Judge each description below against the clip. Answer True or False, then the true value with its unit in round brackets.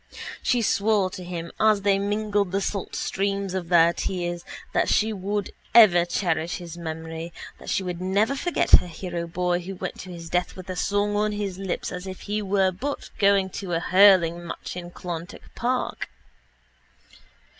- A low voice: False (185 Hz)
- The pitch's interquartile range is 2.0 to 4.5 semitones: True (2.7 semitones)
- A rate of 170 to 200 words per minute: True (175 wpm)